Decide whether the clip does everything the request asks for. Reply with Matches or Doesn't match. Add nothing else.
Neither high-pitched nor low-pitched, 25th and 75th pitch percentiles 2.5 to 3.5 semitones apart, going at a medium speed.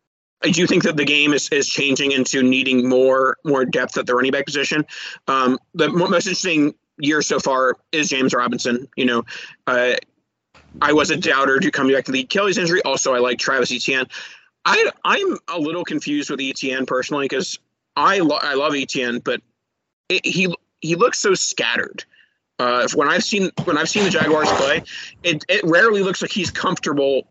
Doesn't match